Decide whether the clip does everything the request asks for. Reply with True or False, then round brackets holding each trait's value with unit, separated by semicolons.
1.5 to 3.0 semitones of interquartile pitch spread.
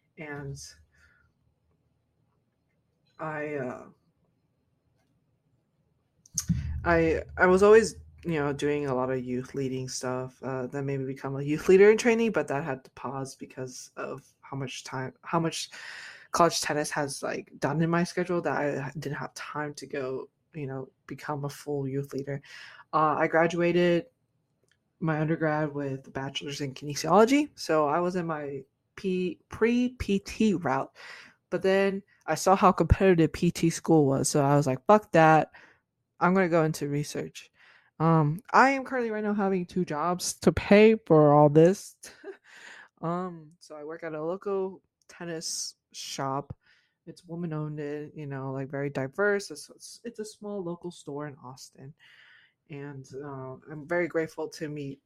False (4.0 semitones)